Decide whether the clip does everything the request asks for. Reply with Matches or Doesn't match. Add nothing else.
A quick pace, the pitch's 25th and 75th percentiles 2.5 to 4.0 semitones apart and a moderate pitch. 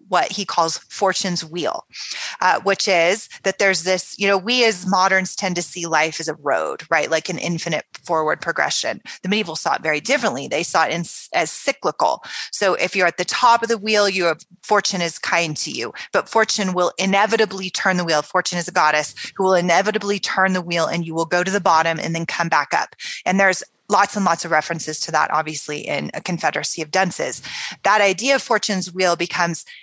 Matches